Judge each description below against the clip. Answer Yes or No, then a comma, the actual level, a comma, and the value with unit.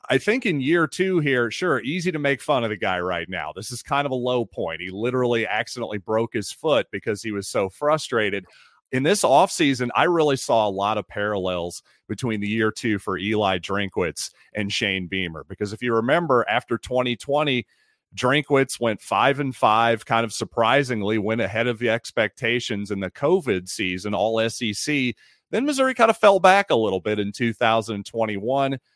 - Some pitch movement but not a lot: Yes, average, 4.4 semitones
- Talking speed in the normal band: Yes, average, 185 wpm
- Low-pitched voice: Yes, low, 115 Hz